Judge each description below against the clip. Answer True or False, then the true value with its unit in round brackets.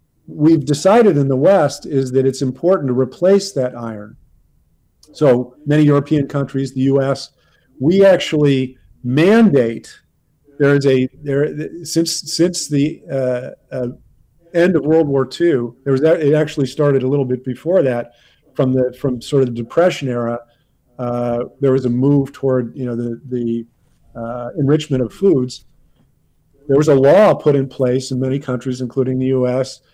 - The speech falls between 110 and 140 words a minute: False (165 wpm)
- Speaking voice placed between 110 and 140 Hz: True (135 Hz)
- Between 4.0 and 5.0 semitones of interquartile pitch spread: False (2.7 semitones)